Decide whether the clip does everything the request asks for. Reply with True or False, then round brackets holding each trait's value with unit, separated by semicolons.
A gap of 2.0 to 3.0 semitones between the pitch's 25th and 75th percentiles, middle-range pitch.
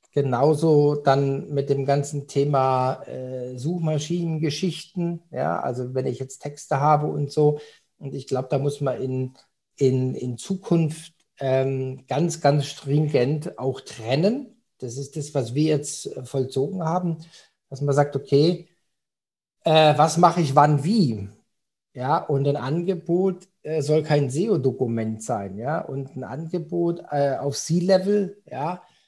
False (3.7 semitones; 145 Hz)